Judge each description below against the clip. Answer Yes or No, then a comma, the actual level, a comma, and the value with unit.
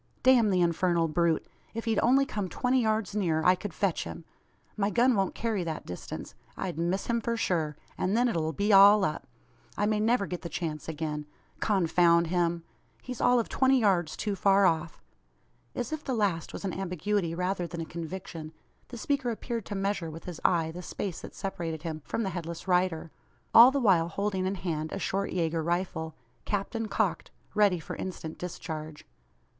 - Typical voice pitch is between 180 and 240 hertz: Yes, medium, 185 Hz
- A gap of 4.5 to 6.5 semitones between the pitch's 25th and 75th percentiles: No, average, 4.1 semitones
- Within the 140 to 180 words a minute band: No, average, 190 wpm